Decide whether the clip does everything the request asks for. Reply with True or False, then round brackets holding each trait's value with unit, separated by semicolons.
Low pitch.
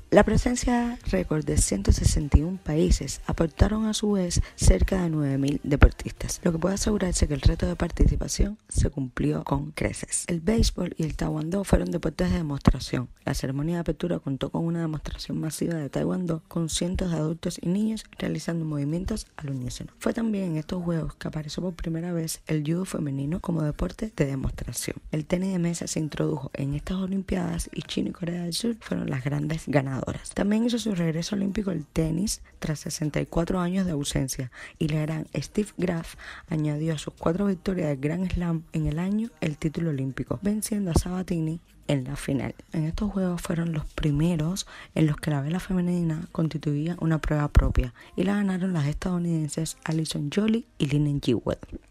False (165 Hz)